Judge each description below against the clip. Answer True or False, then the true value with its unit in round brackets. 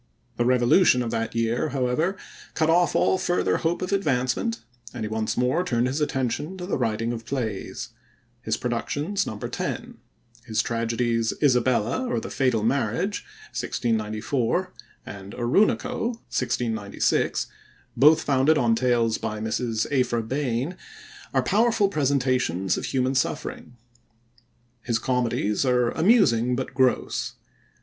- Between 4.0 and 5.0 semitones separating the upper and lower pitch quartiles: True (4.4 semitones)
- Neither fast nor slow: False (130 wpm)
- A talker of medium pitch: False (125 Hz)